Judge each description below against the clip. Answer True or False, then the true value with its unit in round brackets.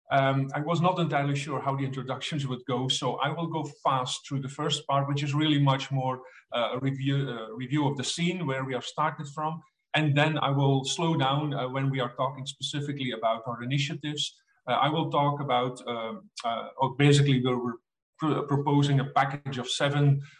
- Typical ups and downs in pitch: False (2.2 semitones)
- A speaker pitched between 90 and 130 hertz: False (140 Hz)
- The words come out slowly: False (205 wpm)